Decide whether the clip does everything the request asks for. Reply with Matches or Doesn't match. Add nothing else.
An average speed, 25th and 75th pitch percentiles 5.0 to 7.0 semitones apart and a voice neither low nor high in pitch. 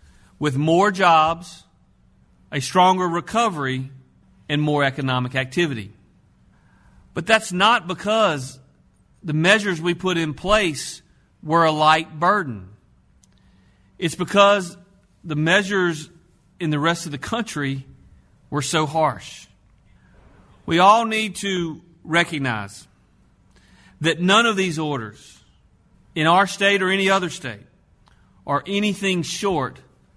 Doesn't match